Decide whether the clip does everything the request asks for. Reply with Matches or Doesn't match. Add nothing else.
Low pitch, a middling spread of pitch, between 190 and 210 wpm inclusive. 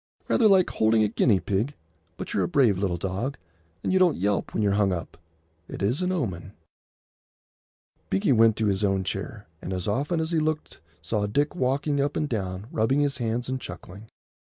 Doesn't match